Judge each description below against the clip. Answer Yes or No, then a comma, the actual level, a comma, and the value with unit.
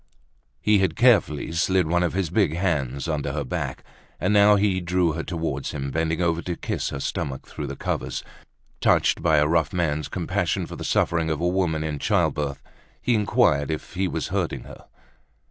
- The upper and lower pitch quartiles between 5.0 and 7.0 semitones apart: No, average, 3.5 semitones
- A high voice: No, very low, 80 Hz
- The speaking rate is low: No, average, 190 wpm